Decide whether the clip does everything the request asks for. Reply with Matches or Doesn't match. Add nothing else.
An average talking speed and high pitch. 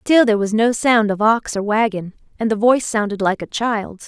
Doesn't match